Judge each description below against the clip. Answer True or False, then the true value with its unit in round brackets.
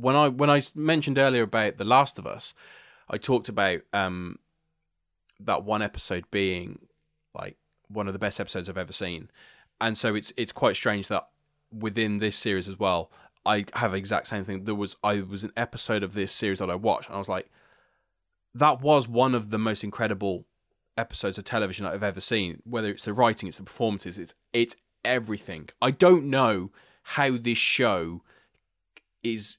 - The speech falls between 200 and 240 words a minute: False (185 wpm)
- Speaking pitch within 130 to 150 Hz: False (105 Hz)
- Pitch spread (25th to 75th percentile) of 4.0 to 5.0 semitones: False (3.5 semitones)